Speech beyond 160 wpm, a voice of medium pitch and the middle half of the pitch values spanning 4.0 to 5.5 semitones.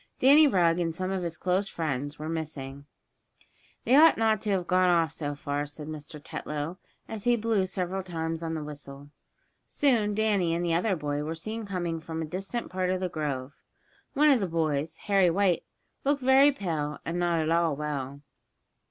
Yes: average, 190 wpm; medium, 170 Hz; average, 4.5 semitones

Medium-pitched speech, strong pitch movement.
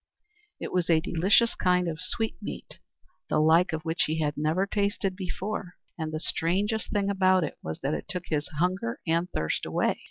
No: medium, 180 Hz; average, 3.7 semitones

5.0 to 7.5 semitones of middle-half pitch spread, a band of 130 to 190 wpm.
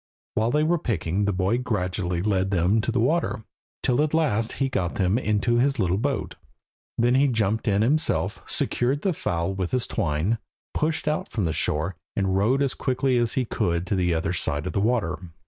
No: wide, 5.6 semitones; average, 200 wpm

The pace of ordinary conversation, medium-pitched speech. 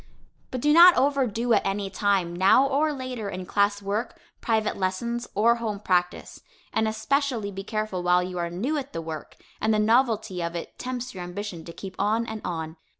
No: average, 195 wpm; high, 210 Hz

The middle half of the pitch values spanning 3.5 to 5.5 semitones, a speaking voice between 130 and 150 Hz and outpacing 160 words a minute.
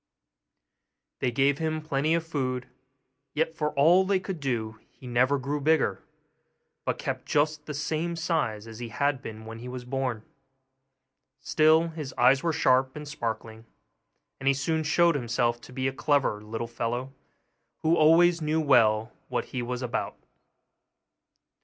No: average, 4.5 semitones; low, 135 Hz; average, 155 wpm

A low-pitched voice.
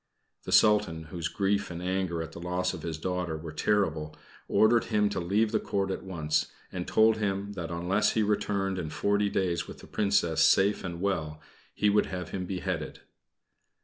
Yes: very low, 95 Hz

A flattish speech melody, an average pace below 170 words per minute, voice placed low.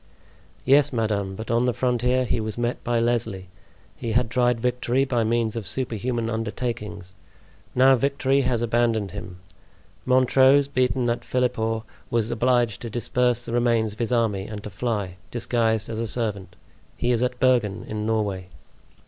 Yes: narrow, 2.3 semitones; average, 160 wpm; low, 115 Hz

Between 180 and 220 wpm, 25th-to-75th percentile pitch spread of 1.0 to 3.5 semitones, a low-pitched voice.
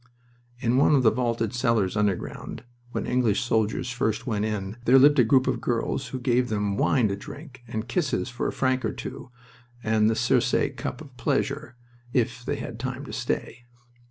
Yes: average, 185 wpm; average, 2.9 semitones; low, 120 Hz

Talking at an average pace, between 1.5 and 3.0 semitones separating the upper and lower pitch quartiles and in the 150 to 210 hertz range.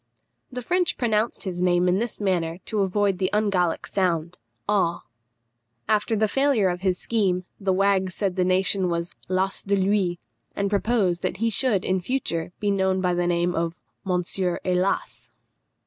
Yes: average, 165 wpm; narrow, 2.5 semitones; high, 190 Hz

